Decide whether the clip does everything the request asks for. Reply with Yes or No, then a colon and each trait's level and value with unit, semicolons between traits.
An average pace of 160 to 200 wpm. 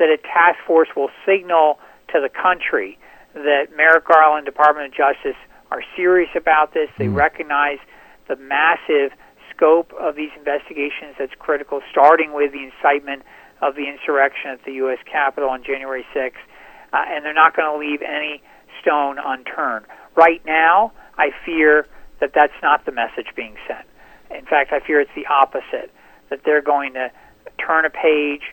Yes: average, 165 wpm